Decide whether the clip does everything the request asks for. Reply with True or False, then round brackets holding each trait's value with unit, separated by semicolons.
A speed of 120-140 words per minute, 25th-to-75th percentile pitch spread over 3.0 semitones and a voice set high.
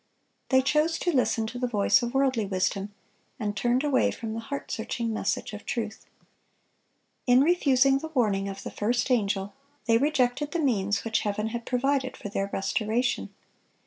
False (170 wpm; 4.1 semitones; 240 Hz)